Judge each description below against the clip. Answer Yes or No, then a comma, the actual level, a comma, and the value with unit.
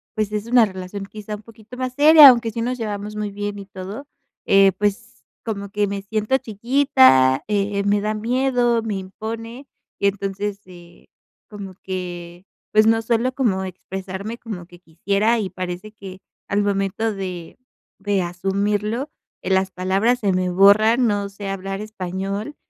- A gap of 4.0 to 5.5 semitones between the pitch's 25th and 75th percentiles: No, average, 2.7 semitones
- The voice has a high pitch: Yes, high, 205 Hz